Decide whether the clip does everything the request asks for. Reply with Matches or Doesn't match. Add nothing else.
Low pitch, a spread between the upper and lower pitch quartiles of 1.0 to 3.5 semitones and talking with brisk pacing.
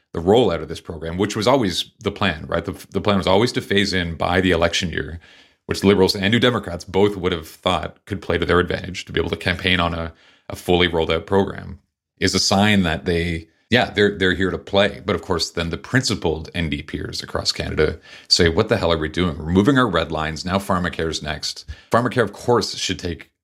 Matches